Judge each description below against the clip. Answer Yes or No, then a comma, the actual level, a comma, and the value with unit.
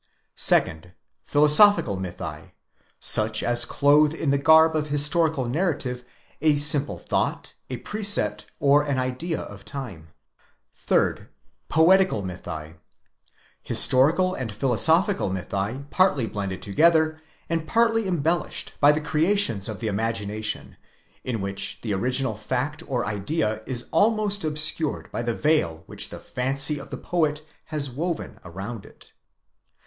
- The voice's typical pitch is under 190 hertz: Yes, medium, 140 Hz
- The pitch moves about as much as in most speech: No, wide, 6.8 semitones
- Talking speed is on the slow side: Yes, slow, 130 wpm